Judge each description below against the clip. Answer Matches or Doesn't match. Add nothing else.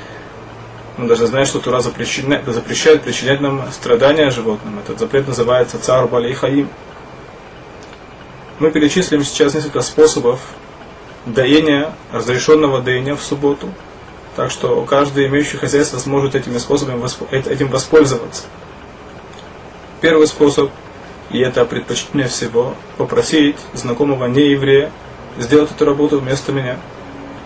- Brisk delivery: Doesn't match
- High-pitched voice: Doesn't match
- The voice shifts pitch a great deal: Doesn't match